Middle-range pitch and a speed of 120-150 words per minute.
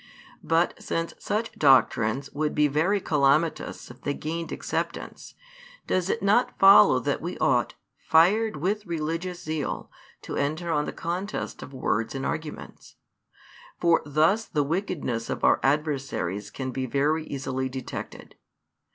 Yes: medium, 155 Hz; average, 140 wpm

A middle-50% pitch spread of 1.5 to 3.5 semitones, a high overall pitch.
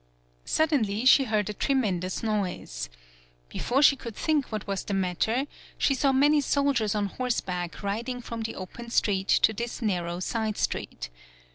No: average, 4.8 semitones; high, 220 Hz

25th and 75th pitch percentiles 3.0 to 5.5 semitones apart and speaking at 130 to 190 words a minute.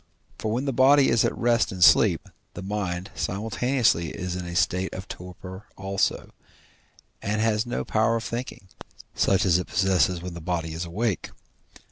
Yes: average, 4.1 semitones; average, 170 wpm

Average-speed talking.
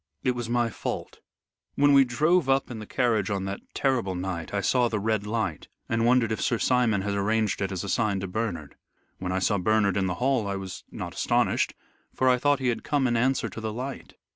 No: fast, 230 wpm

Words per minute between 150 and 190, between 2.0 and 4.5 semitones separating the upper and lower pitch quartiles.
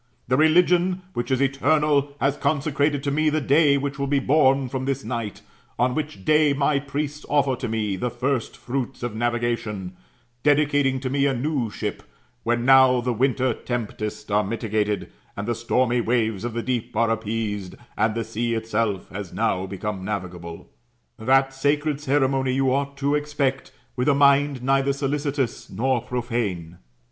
Yes: average, 170 wpm; average, 3.7 semitones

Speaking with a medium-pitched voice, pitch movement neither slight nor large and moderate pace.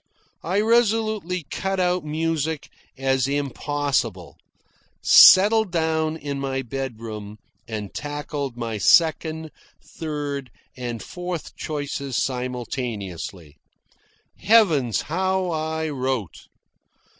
No: medium, 145 Hz; average, 4.7 semitones; slow, 85 wpm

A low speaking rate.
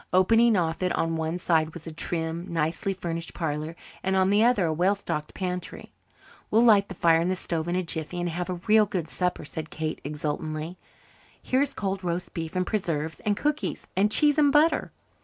No: average, 200 wpm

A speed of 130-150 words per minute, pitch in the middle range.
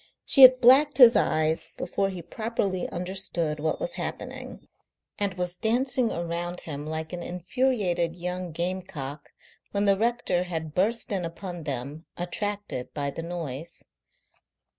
Yes: average, 140 wpm; medium, 180 Hz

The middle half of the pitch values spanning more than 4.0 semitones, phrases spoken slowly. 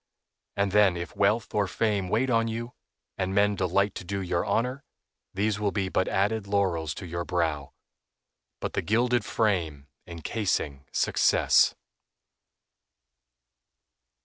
No: average, 3.5 semitones; slow, 130 wpm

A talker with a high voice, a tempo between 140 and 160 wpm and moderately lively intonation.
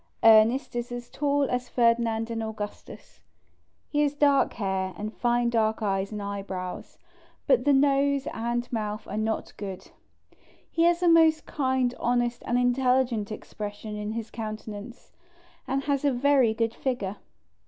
Yes: high, 235 Hz; average, 150 wpm; average, 3.9 semitones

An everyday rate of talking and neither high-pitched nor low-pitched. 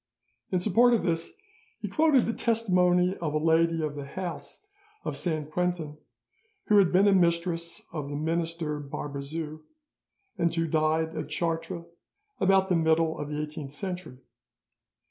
Yes: average, 150 wpm; medium, 165 Hz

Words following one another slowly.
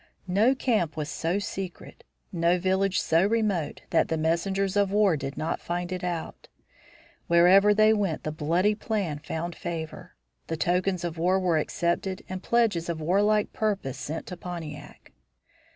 No: average, 155 wpm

